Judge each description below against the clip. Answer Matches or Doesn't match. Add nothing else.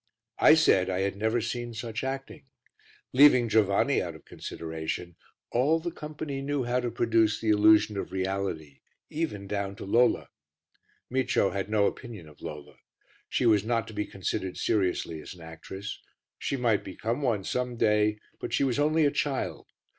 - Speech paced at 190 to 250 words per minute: Doesn't match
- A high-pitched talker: Doesn't match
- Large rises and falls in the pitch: Doesn't match